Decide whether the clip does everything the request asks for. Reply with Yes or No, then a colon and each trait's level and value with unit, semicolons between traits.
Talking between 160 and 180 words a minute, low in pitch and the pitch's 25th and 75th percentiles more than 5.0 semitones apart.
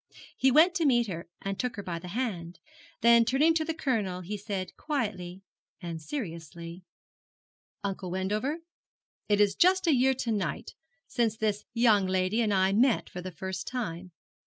No: average, 170 wpm; high, 205 Hz; wide, 5.4 semitones